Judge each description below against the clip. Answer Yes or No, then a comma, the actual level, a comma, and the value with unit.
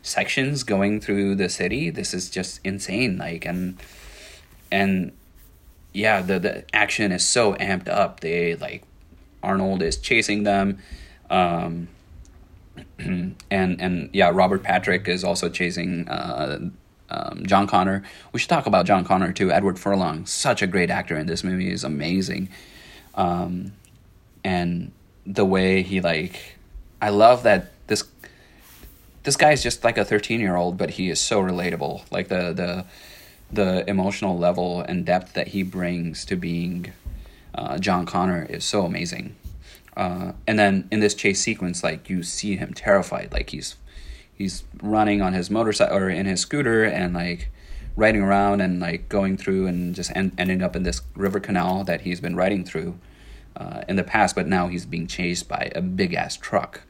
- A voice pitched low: Yes, very low, 90 Hz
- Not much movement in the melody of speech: Yes, narrow, 2.2 semitones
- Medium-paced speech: Yes, average, 165 wpm